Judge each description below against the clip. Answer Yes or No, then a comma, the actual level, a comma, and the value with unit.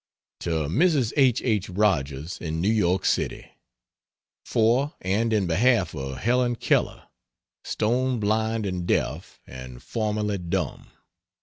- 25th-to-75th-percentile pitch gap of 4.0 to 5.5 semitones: Yes, average, 5.2 semitones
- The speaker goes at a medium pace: No, slow, 120 wpm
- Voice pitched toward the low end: Yes, low, 105 Hz